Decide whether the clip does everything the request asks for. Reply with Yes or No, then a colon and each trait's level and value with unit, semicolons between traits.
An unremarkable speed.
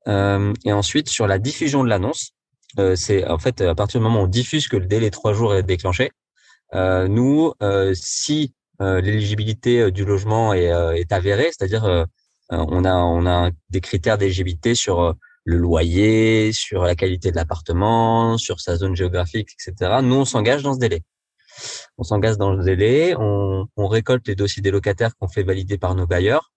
Yes: average, 195 wpm